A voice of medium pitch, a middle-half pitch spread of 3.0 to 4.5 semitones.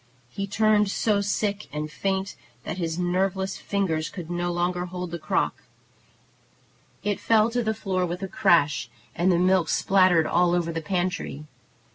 No: medium, 180 Hz; narrow, 2.4 semitones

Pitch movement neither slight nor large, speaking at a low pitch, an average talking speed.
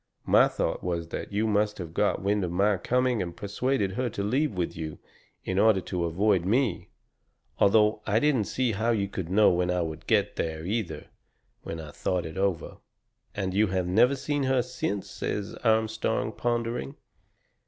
Yes: average, 3.8 semitones; low, 100 Hz; average, 180 wpm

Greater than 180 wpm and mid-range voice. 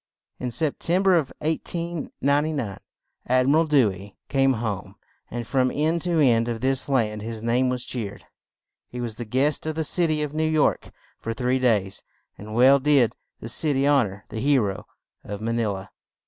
No: average, 200 wpm; low, 130 Hz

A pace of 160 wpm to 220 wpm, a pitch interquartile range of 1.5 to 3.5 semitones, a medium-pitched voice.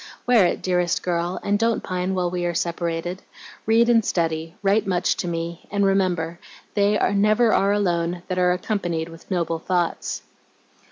Yes: average, 165 wpm; average, 2.9 semitones; medium, 180 Hz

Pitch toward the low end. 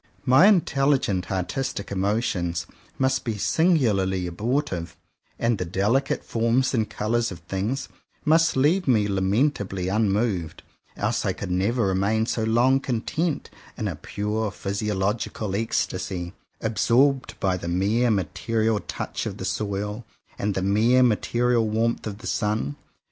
Yes: low, 110 Hz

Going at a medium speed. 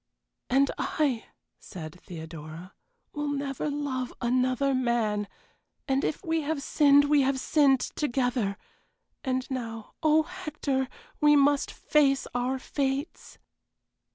No: slow, 115 wpm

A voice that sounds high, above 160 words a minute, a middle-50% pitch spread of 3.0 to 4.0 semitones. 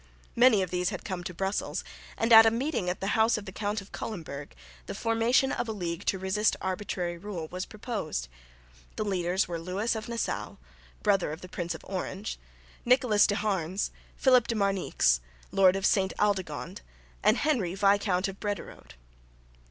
Yes: high, 195 Hz; average, 175 wpm; average, 3.3 semitones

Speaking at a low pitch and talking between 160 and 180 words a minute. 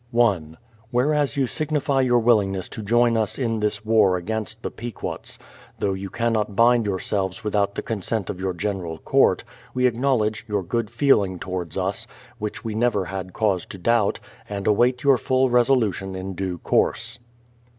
Yes: low, 110 Hz; average, 165 wpm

